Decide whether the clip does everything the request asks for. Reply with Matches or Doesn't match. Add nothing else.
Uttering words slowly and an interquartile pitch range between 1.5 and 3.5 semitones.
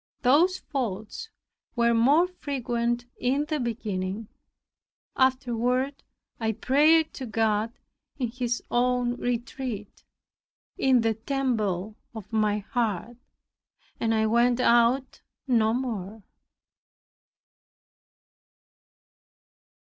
Matches